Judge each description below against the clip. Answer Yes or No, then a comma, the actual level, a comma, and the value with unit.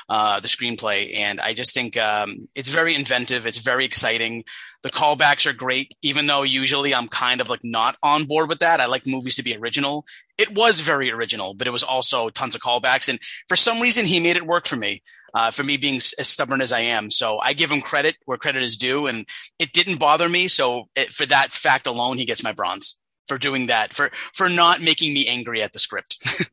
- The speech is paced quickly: Yes, fast, 235 wpm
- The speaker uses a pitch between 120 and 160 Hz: Yes, medium, 140 Hz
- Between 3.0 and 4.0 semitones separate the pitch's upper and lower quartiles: No, average, 4.9 semitones